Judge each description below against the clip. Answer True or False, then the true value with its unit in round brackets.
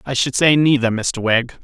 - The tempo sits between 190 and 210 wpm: False (220 wpm)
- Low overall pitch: True (130 Hz)